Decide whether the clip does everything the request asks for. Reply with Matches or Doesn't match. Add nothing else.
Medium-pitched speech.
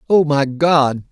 Matches